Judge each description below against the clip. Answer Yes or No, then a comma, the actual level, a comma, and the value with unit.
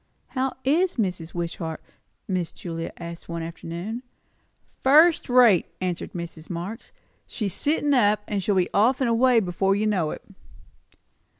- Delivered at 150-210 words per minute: No, slow, 135 wpm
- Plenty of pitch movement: Yes, wide, 6.5 semitones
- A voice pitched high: Yes, high, 195 Hz